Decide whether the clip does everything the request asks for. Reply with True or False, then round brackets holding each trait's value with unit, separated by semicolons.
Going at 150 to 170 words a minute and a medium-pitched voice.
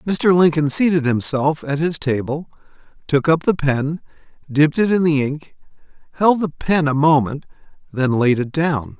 True (165 wpm; 150 Hz)